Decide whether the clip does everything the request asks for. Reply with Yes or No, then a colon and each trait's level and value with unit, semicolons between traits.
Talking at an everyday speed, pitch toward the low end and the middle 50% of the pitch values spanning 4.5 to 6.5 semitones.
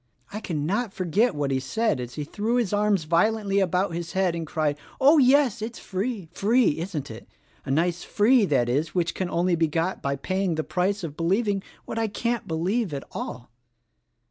No: average, 195 wpm; medium, 185 Hz; average, 5.1 semitones